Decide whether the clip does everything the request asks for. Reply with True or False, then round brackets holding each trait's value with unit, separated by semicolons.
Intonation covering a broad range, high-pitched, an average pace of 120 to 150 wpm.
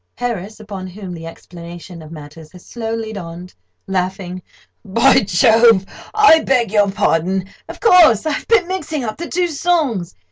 True (5.8 semitones; 205 Hz; 140 wpm)